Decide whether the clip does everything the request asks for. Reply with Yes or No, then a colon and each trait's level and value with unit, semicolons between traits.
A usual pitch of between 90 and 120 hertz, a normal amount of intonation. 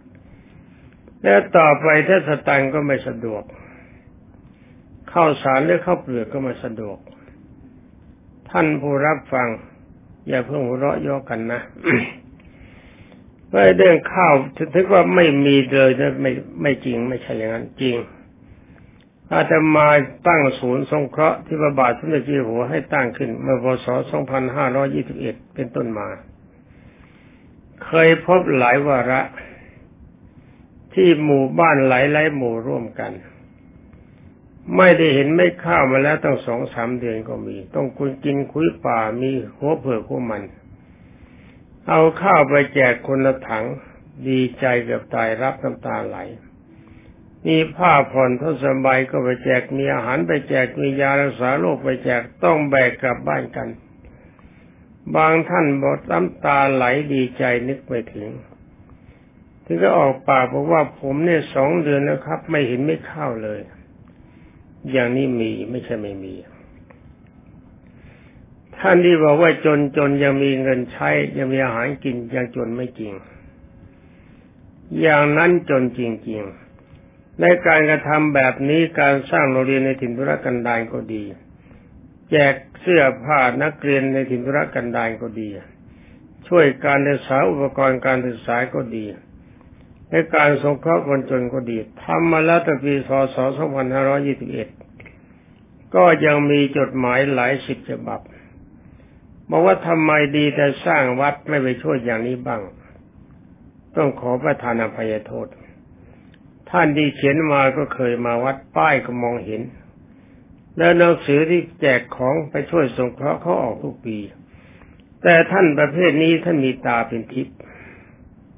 No: low, 135 Hz; average, 3.1 semitones